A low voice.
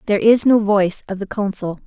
No: high, 205 Hz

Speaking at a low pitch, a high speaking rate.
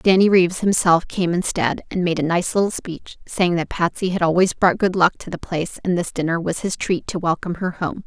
No: medium, 175 Hz; fast, 240 wpm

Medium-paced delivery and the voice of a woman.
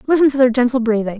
No: fast, 250 wpm; female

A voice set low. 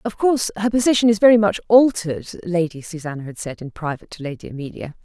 No: medium, 185 Hz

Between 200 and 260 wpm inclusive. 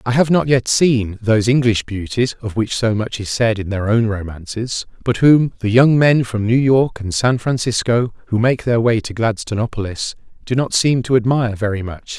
Yes: fast, 205 wpm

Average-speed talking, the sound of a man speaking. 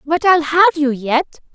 No: average, 195 wpm; female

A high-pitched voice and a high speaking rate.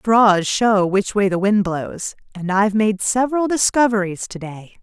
No: high, 205 Hz; average, 160 wpm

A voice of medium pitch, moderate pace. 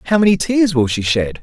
No: medium, 145 Hz; fast, 255 wpm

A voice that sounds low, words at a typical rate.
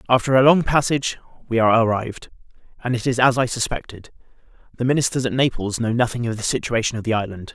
Yes: low, 120 Hz; average, 190 wpm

